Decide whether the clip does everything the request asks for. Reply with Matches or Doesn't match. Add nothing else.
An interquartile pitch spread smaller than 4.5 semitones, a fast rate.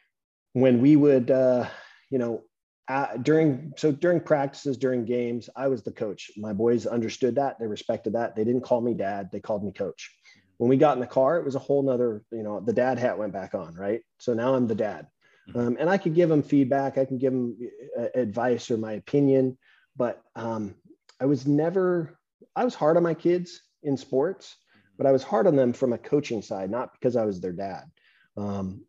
Matches